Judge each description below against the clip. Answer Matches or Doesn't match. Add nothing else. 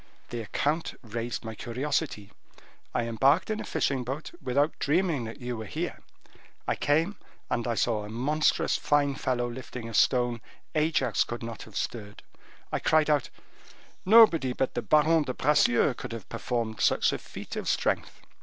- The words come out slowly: Doesn't match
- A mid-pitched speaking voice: Doesn't match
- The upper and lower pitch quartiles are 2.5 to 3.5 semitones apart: Doesn't match